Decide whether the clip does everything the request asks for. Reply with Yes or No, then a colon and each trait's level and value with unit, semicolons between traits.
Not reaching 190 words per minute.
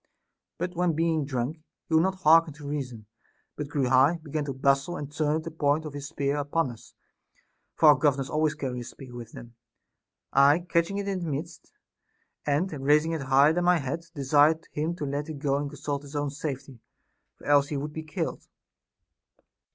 No: average, 195 wpm